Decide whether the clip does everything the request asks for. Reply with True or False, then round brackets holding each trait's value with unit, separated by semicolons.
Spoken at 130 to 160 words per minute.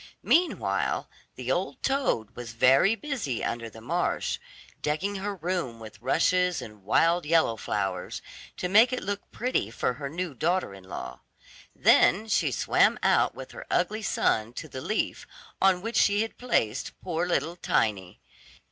True (155 wpm)